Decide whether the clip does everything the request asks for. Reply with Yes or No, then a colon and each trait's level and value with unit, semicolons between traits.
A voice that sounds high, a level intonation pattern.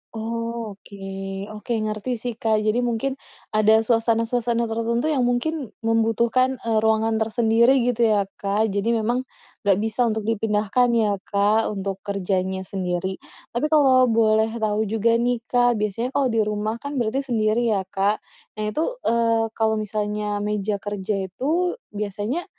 Yes: high, 225 Hz; narrow, 2.2 semitones